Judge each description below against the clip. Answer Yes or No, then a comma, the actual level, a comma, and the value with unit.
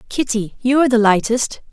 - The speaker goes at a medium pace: Yes, average, 175 wpm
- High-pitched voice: Yes, high, 235 Hz